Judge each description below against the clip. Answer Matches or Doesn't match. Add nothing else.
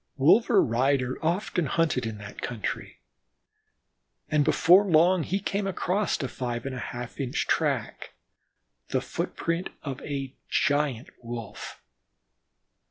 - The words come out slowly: Matches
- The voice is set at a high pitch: Doesn't match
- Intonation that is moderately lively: Doesn't match